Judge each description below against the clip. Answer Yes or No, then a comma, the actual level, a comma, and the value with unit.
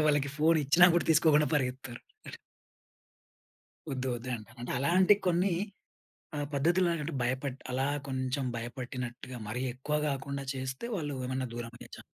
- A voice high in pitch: No, low, 135 Hz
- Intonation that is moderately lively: Yes, average, 3.0 semitones